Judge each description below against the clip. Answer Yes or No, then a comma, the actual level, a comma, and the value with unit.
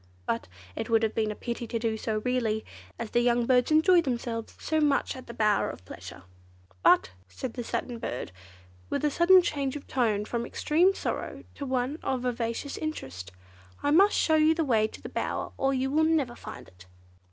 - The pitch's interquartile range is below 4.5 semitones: No, average, 4.8 semitones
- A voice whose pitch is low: No, very high, 250 Hz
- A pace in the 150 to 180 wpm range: No, average, 200 wpm